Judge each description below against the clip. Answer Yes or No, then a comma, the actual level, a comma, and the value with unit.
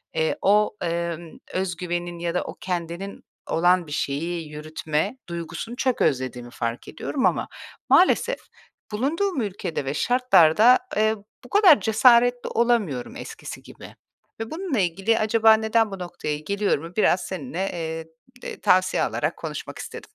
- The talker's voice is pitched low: No, medium, 185 Hz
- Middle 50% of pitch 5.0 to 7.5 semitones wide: Yes, wide, 5.6 semitones